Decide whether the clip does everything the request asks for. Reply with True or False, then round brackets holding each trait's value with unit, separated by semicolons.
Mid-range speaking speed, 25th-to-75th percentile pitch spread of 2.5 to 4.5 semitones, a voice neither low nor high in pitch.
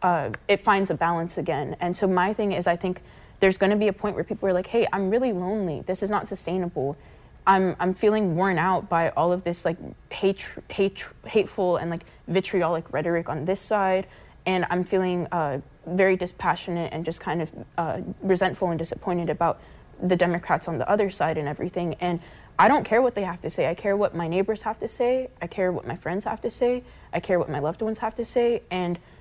False (225 wpm; 2.8 semitones; 180 Hz)